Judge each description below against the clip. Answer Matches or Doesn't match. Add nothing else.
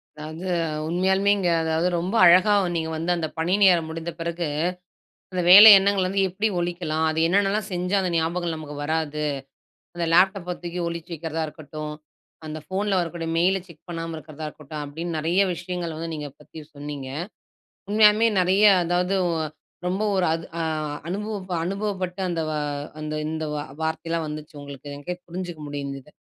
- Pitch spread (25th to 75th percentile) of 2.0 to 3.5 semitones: Matches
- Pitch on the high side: Doesn't match